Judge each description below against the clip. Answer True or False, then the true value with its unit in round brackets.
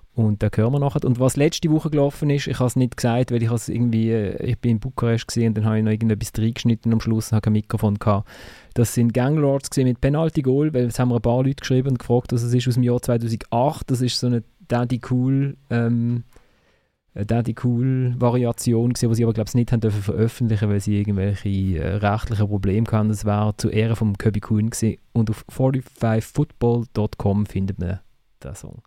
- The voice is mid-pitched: False (115 Hz)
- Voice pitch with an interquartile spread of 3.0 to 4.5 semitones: False (2.5 semitones)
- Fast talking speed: True (210 wpm)